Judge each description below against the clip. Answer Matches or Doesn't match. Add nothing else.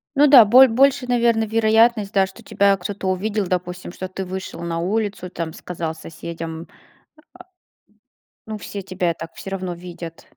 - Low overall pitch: Doesn't match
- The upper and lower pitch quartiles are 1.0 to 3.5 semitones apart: Doesn't match